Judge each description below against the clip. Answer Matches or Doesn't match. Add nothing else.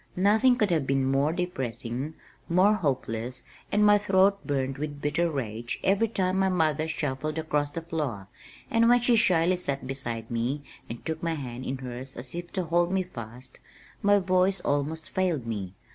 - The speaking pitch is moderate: Matches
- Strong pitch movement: Matches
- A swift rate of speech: Doesn't match